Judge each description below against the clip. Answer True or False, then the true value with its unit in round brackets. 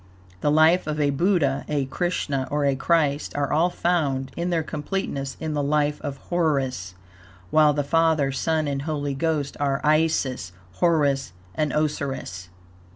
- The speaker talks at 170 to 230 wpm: False (155 wpm)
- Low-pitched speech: False (145 Hz)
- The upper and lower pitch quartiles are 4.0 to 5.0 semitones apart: False (2.5 semitones)